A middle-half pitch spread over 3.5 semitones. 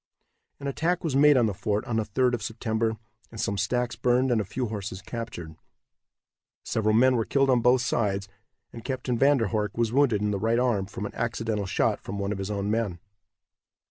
No: average, 3.2 semitones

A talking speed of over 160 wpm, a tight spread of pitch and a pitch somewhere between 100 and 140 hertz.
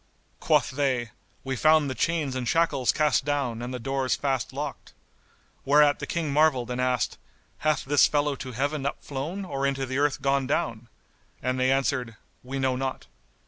Yes: average, 180 wpm; narrow, 2.3 semitones; low, 135 Hz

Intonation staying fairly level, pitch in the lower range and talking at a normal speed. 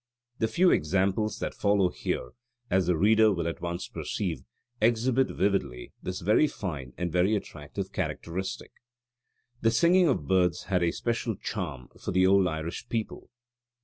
No: average, 4.2 semitones; very low, 95 Hz; average, 150 wpm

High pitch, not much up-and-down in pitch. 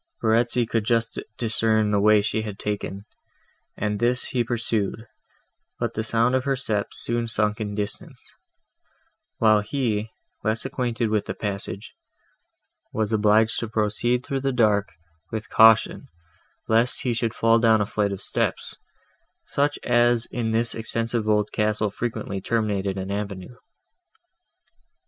No: low, 110 Hz; narrow, 2.0 semitones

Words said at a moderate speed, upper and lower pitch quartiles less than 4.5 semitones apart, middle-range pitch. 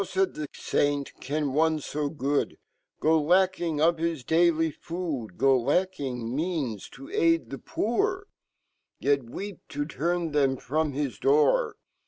No: slow, 130 wpm; average, 3.8 semitones; medium, 155 Hz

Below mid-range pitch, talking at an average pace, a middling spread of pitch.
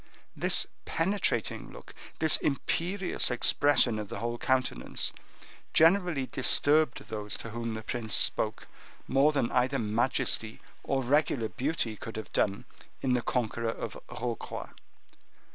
No: low, 125 Hz; slow, 125 wpm; average, 4.4 semitones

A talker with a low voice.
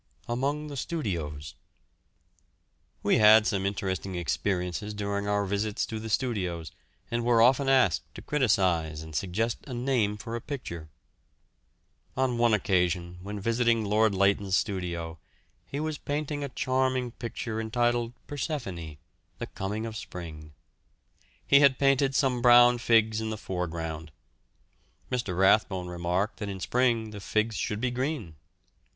Yes: low, 110 Hz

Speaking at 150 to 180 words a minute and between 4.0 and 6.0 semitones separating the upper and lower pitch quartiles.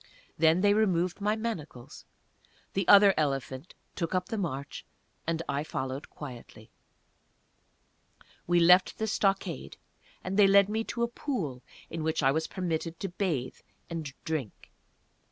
No: average, 140 wpm; average, 5.1 semitones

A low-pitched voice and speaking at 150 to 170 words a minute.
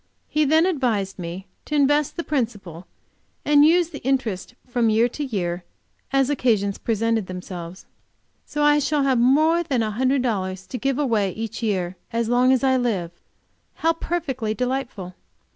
No: high, 245 Hz; average, 160 wpm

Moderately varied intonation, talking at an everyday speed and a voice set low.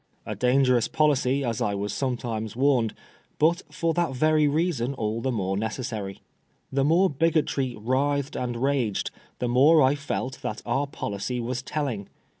Yes: average, 3.8 semitones; average, 155 wpm; low, 130 Hz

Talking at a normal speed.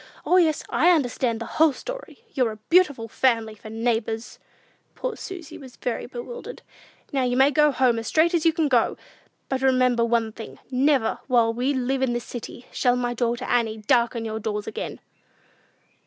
Yes: average, 180 wpm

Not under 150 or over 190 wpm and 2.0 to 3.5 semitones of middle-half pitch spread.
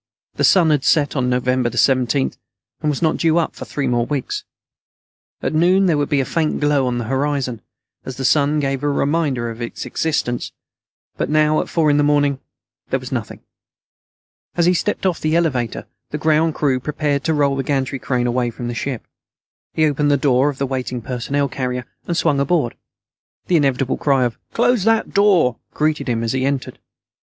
No: average, 200 wpm; average, 3.2 semitones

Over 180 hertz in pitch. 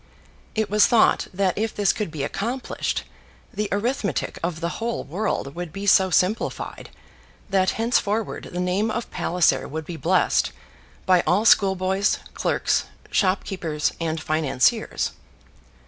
Yes: high, 190 Hz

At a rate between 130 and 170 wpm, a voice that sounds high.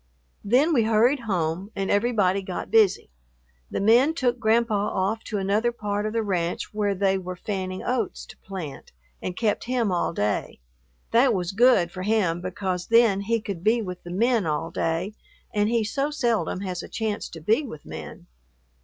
No: average, 180 wpm; high, 205 Hz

